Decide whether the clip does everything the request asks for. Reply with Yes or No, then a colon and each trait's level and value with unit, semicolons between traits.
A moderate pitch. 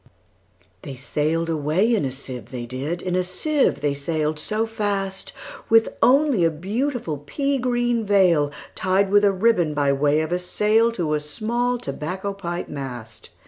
Yes: medium, 180 Hz